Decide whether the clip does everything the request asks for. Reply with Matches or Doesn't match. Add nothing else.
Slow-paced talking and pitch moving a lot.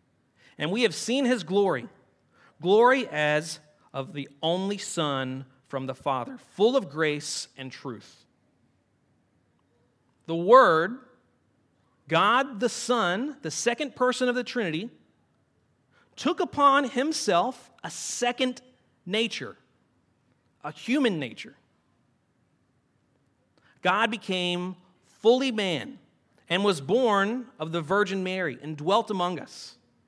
Matches